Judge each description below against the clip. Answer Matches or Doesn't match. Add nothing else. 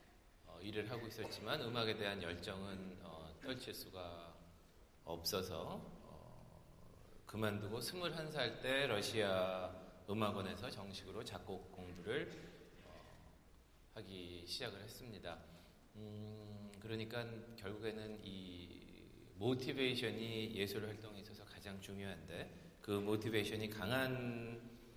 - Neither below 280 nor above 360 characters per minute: Doesn't match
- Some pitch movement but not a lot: Matches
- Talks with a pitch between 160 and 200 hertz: Doesn't match